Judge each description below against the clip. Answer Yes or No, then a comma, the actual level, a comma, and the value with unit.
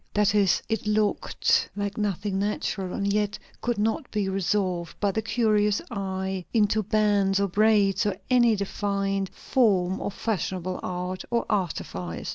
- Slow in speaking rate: No, average, 145 wpm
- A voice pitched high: Yes, high, 200 Hz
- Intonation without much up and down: Yes, narrow, 1.8 semitones